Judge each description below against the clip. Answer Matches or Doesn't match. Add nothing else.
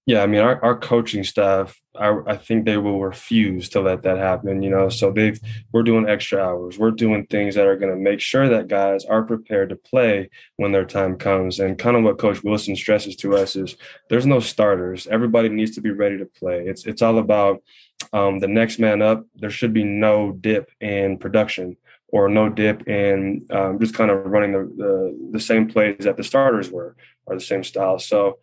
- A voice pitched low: Matches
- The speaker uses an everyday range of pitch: Doesn't match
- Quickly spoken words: Matches